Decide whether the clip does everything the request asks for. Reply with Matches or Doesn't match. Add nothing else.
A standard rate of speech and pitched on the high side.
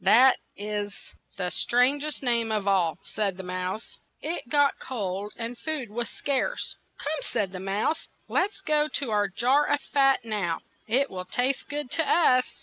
Matches